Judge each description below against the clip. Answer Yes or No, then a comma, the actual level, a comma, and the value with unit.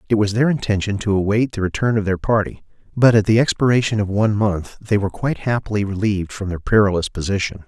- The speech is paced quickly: Yes, fast, 210 wpm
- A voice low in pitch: Yes, low, 105 Hz